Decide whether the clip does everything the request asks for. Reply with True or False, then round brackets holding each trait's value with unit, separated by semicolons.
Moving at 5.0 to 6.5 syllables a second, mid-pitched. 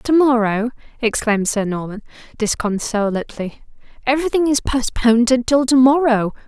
False (5.3 syllables/s; 240 Hz)